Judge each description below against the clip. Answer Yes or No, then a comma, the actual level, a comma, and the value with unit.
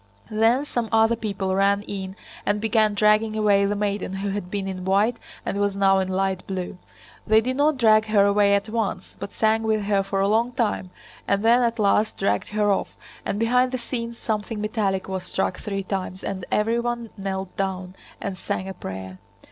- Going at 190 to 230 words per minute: Yes, average, 195 wpm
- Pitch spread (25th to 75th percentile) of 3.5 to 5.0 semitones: No, narrow, 2.5 semitones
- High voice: Yes, high, 205 Hz